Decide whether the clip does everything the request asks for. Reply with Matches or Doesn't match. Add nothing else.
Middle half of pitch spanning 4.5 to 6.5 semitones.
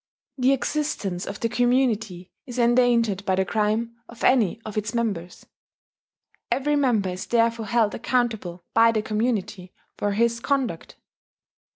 Doesn't match